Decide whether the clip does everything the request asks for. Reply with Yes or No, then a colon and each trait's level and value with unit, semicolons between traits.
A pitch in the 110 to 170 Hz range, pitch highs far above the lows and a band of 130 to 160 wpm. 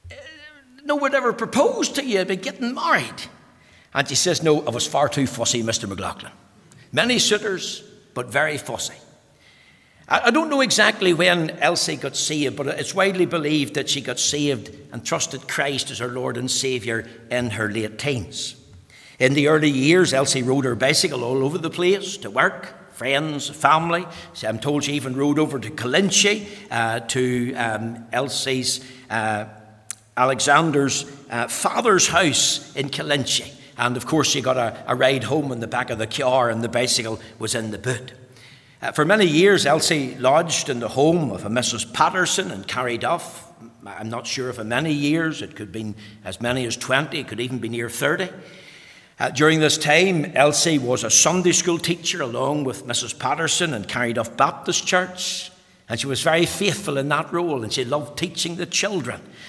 No: medium, 140 Hz; wide, 5.7 semitones; average, 180 wpm